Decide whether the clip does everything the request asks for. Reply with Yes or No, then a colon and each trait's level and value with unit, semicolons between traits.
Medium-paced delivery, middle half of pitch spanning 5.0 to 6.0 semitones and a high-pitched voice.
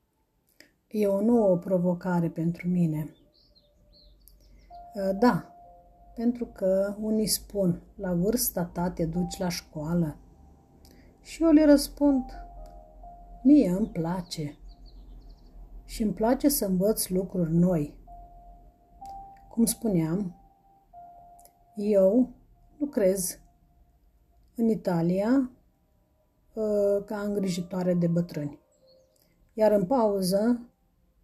No: slow, 85 wpm; average, 5.3 semitones; high, 195 Hz